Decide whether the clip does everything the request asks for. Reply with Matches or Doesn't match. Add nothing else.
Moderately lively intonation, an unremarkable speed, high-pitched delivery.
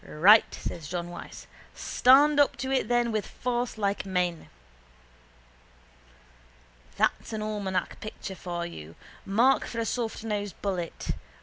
Doesn't match